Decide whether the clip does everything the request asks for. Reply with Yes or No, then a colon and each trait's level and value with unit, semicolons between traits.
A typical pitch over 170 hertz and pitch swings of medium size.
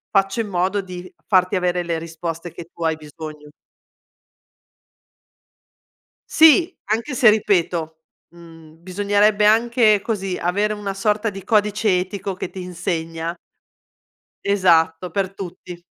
Yes: medium, 185 Hz; average, 3.6 semitones